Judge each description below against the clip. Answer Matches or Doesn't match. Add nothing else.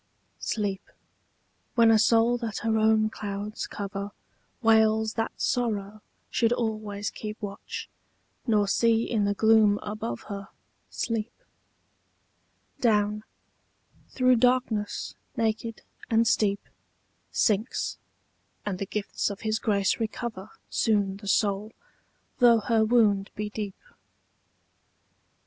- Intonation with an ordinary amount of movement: Doesn't match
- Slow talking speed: Matches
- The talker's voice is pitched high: Matches